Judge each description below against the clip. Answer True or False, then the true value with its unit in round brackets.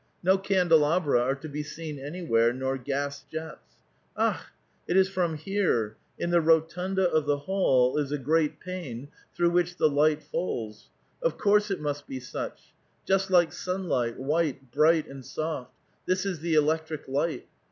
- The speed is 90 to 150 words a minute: False (170 wpm)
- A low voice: False (155 Hz)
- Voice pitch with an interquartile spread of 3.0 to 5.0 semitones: True (4.1 semitones)